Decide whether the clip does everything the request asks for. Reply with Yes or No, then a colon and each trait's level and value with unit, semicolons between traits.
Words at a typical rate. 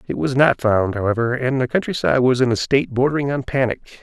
No: fast, 225 wpm